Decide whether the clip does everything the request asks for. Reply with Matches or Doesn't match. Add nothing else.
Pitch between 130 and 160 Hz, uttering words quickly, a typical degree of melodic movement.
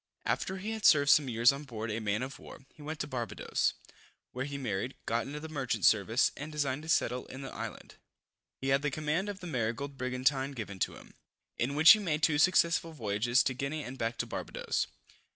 Matches